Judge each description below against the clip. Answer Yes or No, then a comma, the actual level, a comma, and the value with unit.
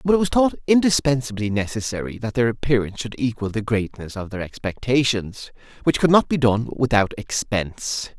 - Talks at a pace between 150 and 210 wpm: Yes, average, 170 wpm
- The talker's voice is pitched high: No, low, 120 Hz